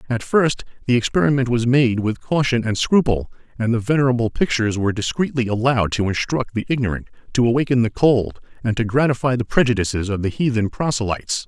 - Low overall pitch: Yes, low, 120 Hz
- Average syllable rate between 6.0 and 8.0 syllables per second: Yes, 6.2 syllables/s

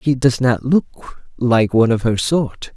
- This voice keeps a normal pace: Yes, average, 195 wpm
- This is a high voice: No, low, 125 Hz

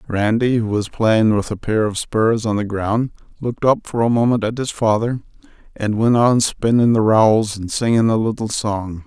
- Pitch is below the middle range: Yes, low, 110 Hz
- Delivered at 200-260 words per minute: Yes, fast, 205 wpm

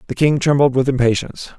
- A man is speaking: Yes, male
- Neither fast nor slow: Yes, average, 190 wpm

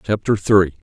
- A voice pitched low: Yes, low, 100 Hz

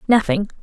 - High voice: Yes, high, 220 Hz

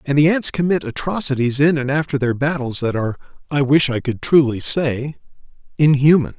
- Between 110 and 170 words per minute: Yes, average, 160 wpm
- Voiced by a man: Yes, male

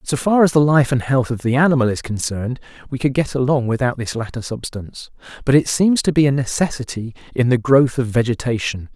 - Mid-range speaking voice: No, low, 130 Hz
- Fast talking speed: Yes, fast, 215 wpm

